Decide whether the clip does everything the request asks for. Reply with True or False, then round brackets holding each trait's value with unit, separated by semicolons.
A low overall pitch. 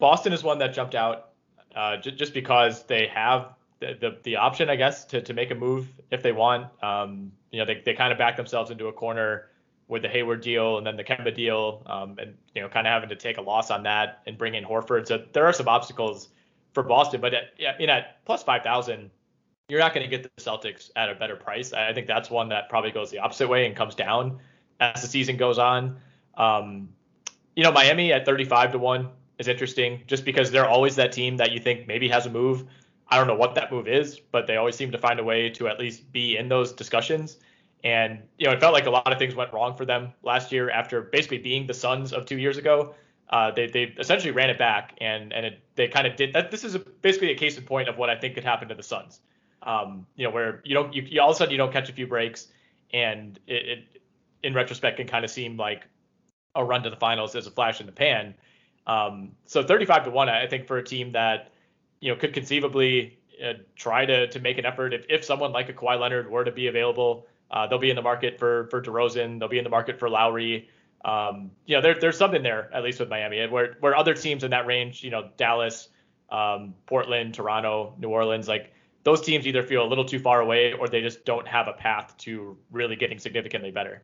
True (120 Hz)